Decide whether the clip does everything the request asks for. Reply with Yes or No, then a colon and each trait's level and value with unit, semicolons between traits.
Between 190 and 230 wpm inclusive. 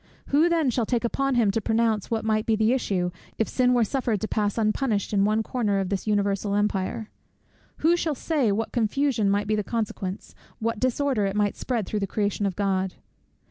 Yes: fast, 205 wpm